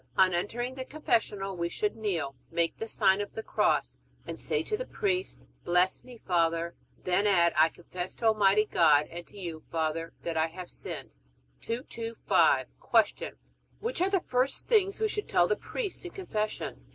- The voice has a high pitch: Yes, high, 205 Hz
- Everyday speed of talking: Yes, average, 175 wpm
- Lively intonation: Yes, wide, 7.0 semitones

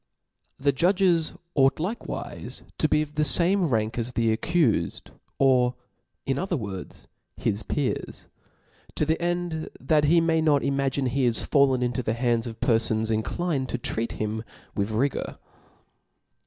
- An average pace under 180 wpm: Yes, average, 150 wpm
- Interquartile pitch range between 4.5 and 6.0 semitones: Yes, average, 5.3 semitones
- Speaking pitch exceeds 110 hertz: Yes, low, 135 Hz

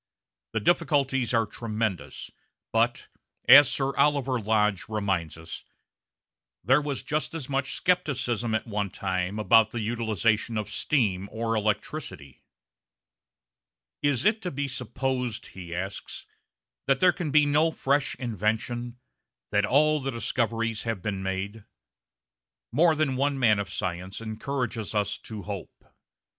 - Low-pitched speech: Yes, low, 115 Hz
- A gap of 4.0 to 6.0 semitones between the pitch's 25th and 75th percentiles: Yes, average, 4.8 semitones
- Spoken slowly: Yes, slow, 130 wpm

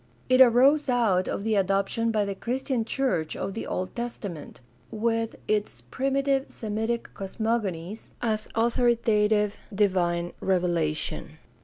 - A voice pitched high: Yes, high, 215 Hz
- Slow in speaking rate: Yes, slow, 120 wpm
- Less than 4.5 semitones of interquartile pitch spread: Yes, average, 3.8 semitones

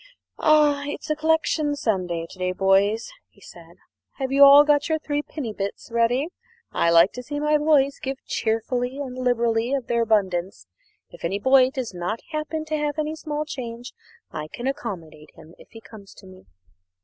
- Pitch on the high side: Yes, very high, 250 Hz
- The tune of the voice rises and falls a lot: Yes, wide, 6.5 semitones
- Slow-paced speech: No, average, 180 wpm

